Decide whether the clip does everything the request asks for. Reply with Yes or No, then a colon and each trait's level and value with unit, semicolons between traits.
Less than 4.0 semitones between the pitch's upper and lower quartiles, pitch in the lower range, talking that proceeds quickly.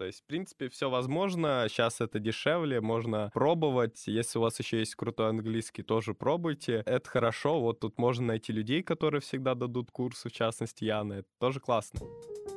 Yes: average, 3.5 semitones; low, 120 Hz; fast, 175 wpm